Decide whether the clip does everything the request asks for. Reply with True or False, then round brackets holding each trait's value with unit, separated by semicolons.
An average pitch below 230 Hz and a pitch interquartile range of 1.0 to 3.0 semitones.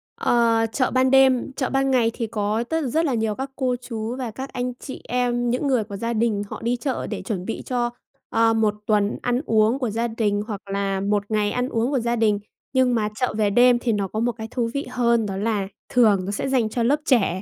False (235 Hz; 2.7 semitones)